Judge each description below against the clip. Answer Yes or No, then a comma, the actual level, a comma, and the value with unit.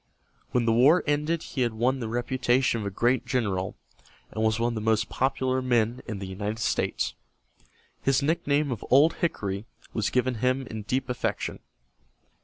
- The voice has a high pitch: No, low, 120 Hz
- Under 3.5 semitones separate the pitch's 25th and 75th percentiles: Yes, average, 3.0 semitones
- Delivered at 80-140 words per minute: No, average, 175 wpm